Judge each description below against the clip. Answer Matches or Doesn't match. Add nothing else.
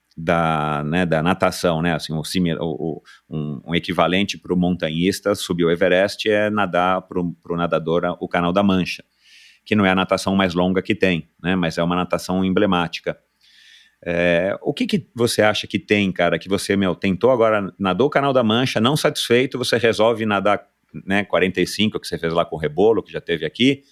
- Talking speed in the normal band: Doesn't match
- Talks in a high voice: Doesn't match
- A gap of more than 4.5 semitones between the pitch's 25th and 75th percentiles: Doesn't match